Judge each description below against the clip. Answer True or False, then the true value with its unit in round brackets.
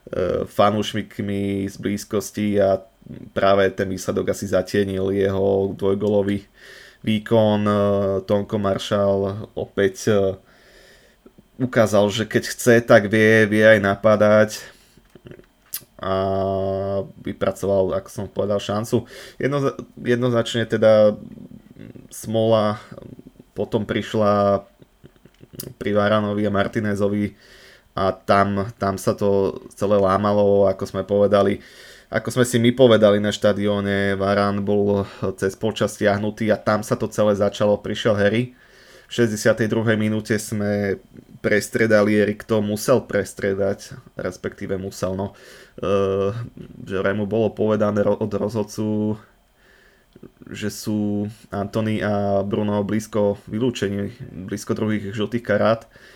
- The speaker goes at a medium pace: False (105 wpm)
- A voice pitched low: True (105 Hz)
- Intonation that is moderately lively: False (1.7 semitones)